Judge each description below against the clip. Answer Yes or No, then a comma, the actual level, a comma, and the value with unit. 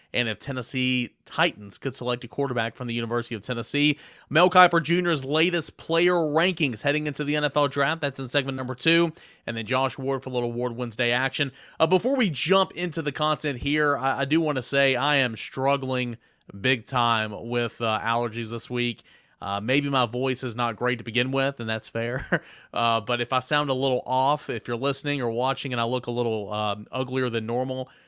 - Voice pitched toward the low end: Yes, low, 130 Hz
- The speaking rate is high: Yes, fast, 210 wpm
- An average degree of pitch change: Yes, average, 3.6 semitones